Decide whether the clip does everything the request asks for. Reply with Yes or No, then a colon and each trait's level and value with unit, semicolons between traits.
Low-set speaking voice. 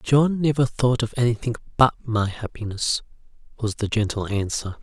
Yes: low, 115 Hz